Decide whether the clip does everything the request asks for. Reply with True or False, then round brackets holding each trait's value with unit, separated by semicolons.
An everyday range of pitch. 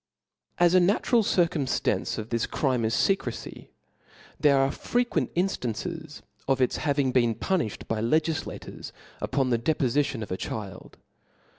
False (6.3 semitones)